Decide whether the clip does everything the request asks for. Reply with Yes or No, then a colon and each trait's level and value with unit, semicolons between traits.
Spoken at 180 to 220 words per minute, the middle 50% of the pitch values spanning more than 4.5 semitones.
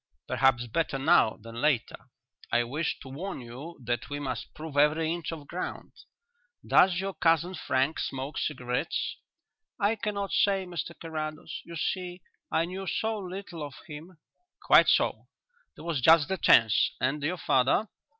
No: average, 155 wpm; average, 5.1 semitones